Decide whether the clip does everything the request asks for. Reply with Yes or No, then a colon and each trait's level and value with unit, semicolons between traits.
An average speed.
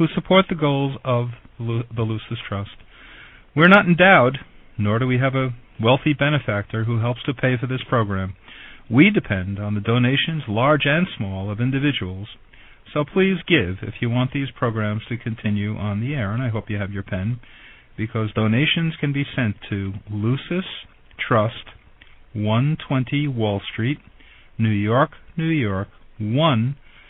Yes: average, 160 wpm